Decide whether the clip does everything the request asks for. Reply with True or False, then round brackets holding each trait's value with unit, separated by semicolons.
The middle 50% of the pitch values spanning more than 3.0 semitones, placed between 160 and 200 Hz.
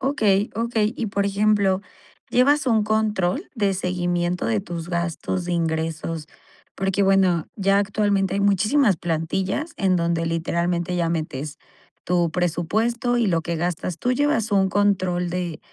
True (3.5 semitones; 185 Hz)